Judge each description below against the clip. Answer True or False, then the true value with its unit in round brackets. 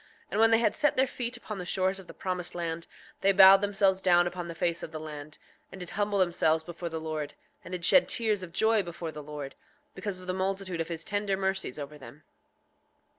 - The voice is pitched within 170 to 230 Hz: True (185 Hz)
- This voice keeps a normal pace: False (225 wpm)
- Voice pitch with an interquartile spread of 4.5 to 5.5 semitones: False (3.2 semitones)